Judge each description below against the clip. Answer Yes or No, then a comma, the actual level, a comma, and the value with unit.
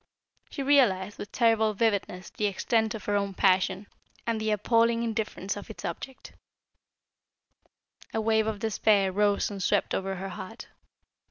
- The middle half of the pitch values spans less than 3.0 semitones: Yes, narrow, 2.4 semitones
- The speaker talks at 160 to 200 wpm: No, average, 150 wpm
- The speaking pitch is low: No, high, 210 Hz